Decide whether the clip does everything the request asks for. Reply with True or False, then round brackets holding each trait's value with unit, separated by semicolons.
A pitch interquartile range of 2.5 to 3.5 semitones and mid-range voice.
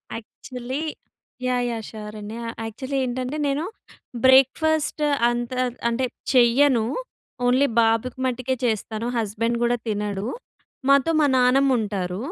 False (2.8 semitones; 245 Hz)